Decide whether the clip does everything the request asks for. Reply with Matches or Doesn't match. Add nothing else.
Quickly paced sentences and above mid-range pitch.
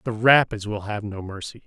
Doesn't match